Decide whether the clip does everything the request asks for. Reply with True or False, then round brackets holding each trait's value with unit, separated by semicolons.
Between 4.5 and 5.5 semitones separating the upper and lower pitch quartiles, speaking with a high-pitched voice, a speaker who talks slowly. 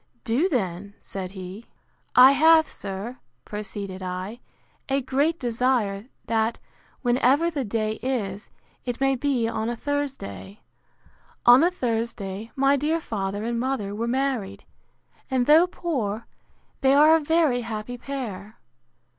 True (4.8 semitones; 240 Hz; 130 wpm)